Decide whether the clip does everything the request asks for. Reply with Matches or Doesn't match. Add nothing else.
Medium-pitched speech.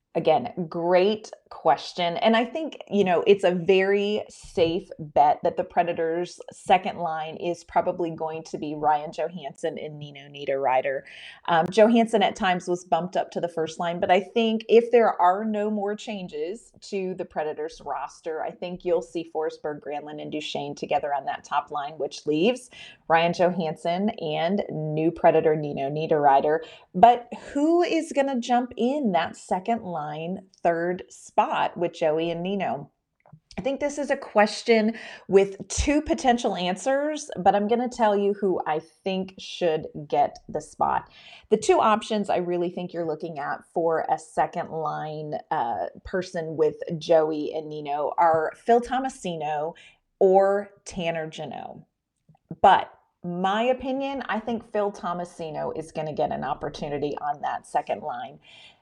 Matches